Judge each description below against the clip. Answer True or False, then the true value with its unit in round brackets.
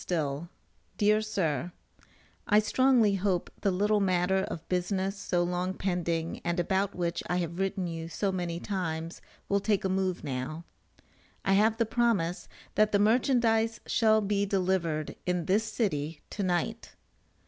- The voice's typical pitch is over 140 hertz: True (190 Hz)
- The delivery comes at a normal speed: True (150 wpm)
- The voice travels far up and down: False (3.3 semitones)